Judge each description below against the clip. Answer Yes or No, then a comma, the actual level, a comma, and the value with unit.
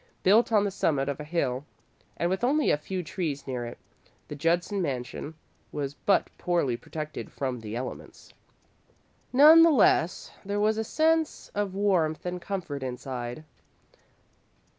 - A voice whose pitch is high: No, medium, 170 Hz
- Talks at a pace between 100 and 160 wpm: Yes, average, 150 wpm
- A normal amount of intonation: No, wide, 6.7 semitones